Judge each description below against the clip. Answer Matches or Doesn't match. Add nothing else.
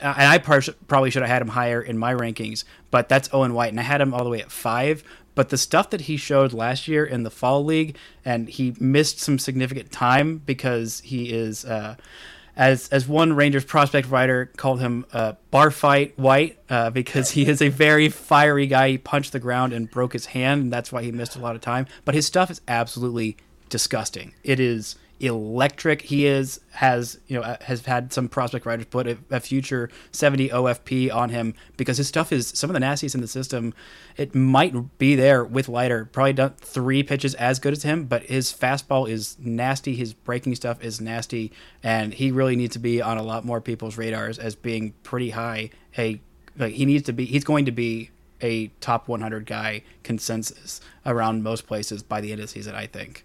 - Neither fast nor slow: Doesn't match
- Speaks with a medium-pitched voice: Doesn't match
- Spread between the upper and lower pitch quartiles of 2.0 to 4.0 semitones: Matches